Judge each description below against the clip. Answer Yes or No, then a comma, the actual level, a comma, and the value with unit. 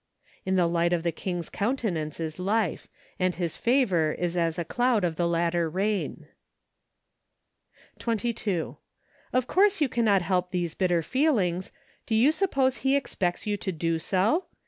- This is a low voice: No, medium, 185 Hz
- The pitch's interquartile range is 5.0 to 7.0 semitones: Yes, wide, 5.5 semitones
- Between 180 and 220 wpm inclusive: No, average, 160 wpm